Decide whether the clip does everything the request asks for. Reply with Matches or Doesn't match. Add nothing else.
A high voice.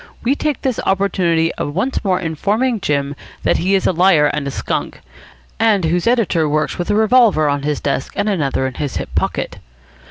Doesn't match